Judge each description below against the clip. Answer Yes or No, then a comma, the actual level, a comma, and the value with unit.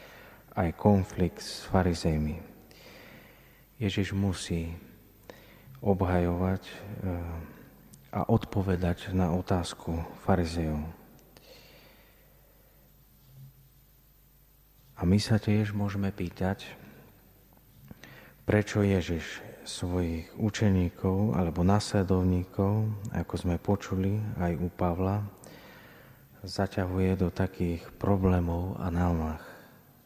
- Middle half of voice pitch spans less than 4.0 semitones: Yes, average, 2.7 semitones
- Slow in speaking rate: Yes, slow, 70 wpm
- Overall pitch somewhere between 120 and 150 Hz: No, very low, 95 Hz